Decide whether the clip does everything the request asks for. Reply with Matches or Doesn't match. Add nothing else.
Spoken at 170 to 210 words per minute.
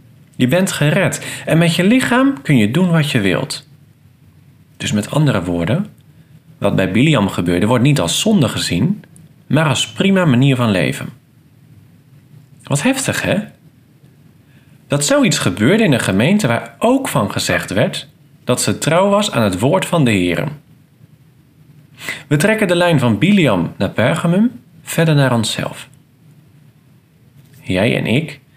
Doesn't match